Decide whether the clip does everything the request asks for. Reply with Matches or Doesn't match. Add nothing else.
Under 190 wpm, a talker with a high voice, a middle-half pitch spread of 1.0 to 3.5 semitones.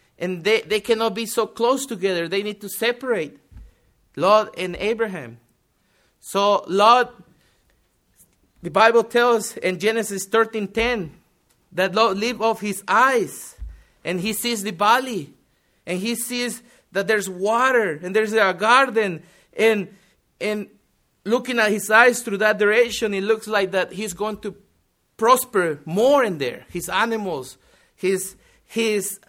Matches